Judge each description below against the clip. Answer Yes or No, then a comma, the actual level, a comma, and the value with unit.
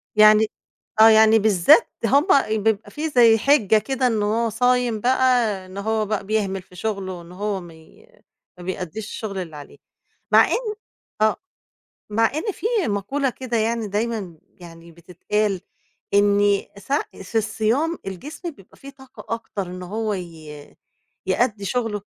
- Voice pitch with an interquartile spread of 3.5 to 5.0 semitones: Yes, average, 3.8 semitones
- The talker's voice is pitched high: Yes, high, 215 Hz